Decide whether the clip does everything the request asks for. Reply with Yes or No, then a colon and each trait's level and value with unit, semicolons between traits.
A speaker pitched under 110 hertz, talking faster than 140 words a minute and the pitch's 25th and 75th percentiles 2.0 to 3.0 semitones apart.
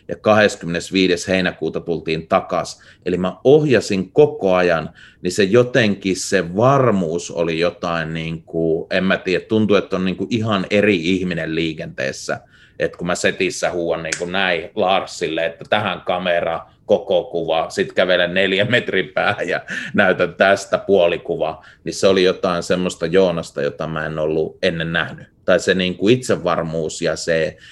Yes: very low, 90 Hz; fast, 155 wpm; average, 2.7 semitones